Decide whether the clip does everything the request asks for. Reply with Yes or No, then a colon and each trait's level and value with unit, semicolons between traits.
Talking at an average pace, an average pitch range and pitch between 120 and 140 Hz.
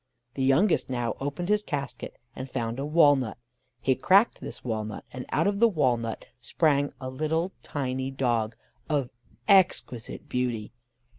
Yes: average, 145 wpm; average, 4.3 semitones; low, 135 Hz